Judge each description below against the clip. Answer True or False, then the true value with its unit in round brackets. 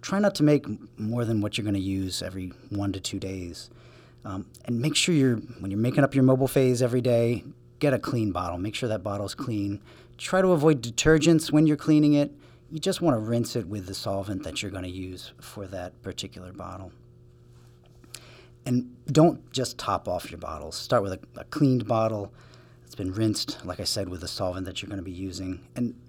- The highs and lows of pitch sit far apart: False (4.5 semitones)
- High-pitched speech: False (120 Hz)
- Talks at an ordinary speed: False (215 wpm)